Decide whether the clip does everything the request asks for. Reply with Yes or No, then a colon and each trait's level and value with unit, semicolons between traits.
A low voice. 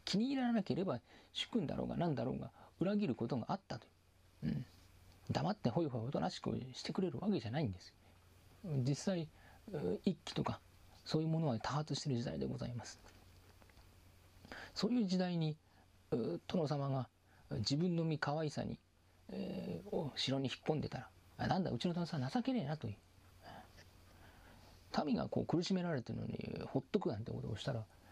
Yes: low, 120 Hz